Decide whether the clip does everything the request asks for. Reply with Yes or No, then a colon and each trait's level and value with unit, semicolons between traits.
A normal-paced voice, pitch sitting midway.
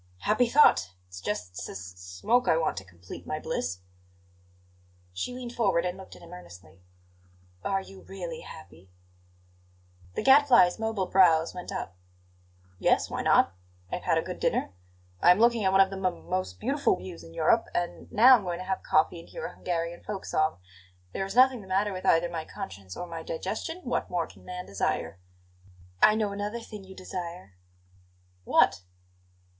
Yes: average, 180 wpm; medium, 180 Hz